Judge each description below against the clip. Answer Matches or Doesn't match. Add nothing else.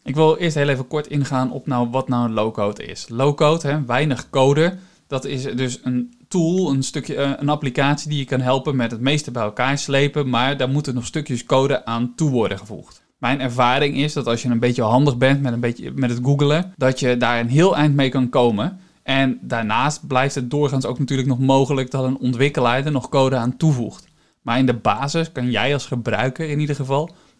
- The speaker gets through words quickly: Matches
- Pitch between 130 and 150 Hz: Matches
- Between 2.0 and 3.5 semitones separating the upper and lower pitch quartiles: Matches